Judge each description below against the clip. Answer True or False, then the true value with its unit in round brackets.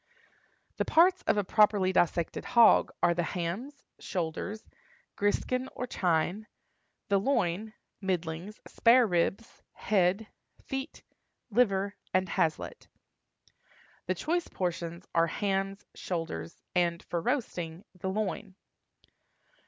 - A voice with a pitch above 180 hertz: True (190 Hz)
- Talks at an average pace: False (105 wpm)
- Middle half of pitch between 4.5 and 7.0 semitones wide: False (4.1 semitones)